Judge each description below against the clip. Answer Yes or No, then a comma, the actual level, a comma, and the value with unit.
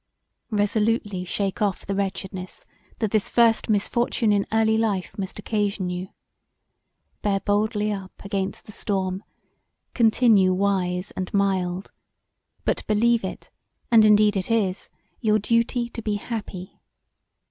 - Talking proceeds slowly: Yes, slow, 125 wpm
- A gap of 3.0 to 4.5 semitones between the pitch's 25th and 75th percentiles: No, narrow, 2.5 semitones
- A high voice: Yes, high, 205 Hz